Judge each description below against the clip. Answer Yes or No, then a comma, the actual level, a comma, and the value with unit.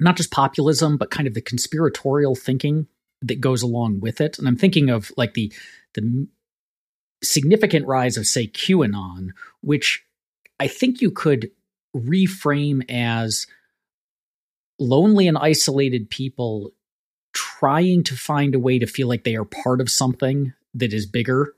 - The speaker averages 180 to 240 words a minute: No, average, 145 wpm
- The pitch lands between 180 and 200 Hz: No, low, 135 Hz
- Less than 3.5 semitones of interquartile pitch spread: No, average, 4.2 semitones